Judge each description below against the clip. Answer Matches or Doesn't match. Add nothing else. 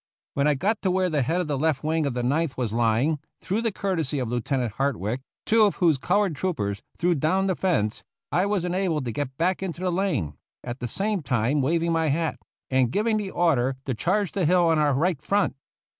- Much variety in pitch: Matches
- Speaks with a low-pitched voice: Doesn't match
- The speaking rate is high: Matches